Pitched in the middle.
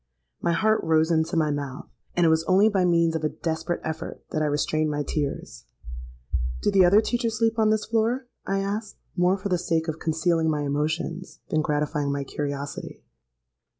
Yes: medium, 160 Hz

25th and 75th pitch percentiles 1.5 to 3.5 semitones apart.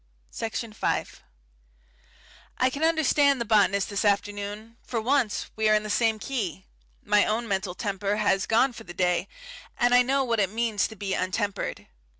Yes: average, 2.9 semitones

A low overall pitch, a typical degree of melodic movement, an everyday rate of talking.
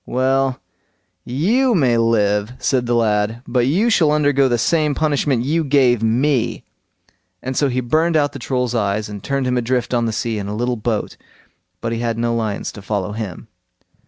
Yes: low, 125 Hz; average, 3.6 semitones; average, 190 wpm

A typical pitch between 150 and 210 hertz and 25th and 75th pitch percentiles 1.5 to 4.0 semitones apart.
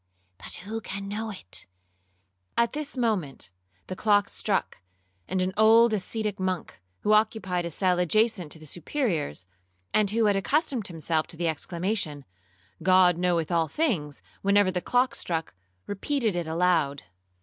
No: medium, 185 Hz; average, 4.5 semitones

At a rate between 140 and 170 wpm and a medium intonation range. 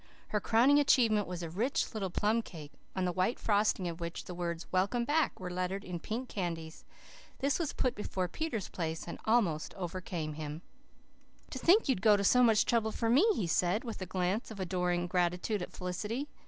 No: average, 200 wpm; average, 4.6 semitones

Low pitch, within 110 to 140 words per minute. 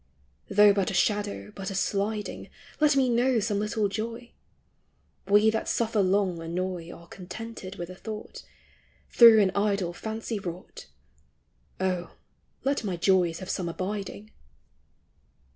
No: high, 200 Hz; slow, 135 wpm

